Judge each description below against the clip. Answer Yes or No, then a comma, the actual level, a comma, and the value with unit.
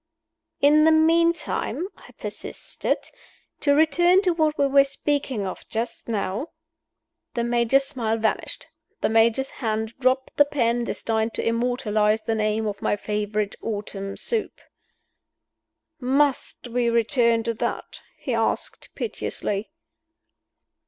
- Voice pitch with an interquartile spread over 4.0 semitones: Yes, average, 4.5 semitones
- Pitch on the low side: No, high, 235 Hz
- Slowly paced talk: Yes, slow, 125 wpm